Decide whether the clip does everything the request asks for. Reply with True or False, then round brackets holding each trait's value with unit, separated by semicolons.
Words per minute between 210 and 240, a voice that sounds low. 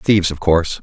True (220 wpm; 85 Hz)